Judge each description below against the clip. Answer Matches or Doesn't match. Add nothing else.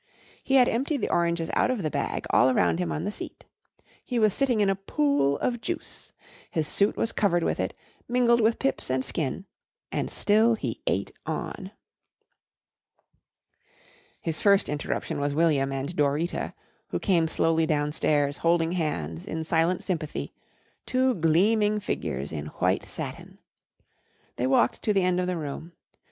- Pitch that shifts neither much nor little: Doesn't match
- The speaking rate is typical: Matches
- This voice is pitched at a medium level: Matches